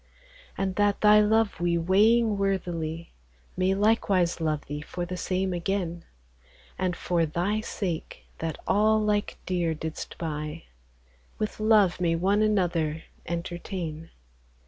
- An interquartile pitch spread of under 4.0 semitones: Yes, average, 3.6 semitones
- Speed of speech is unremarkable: No, slow, 125 wpm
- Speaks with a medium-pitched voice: Yes, medium, 180 Hz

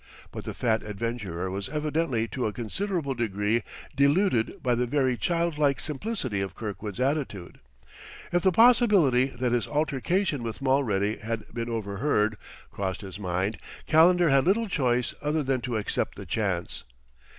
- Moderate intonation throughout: No, wide, 6.1 semitones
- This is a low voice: Yes, low, 125 Hz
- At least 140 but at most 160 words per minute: Yes, average, 150 wpm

